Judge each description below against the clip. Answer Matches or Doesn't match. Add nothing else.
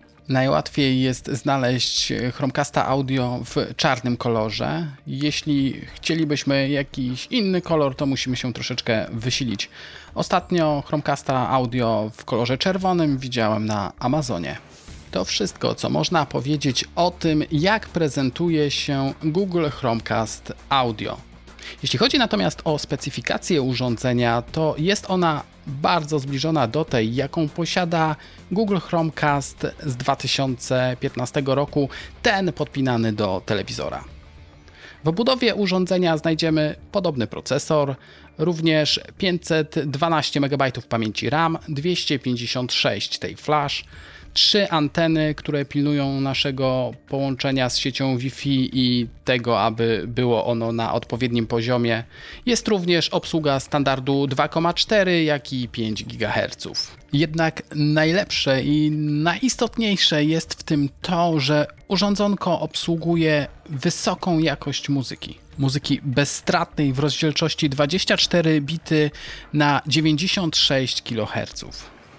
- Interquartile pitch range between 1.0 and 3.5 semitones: Doesn't match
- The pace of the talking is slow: Matches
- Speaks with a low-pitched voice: Doesn't match